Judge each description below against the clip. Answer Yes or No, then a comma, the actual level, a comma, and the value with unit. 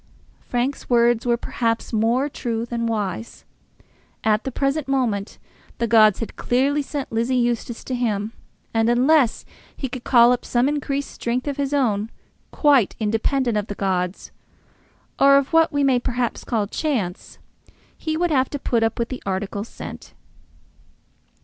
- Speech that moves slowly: No, average, 155 wpm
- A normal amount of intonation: Yes, average, 3.4 semitones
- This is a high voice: Yes, high, 240 Hz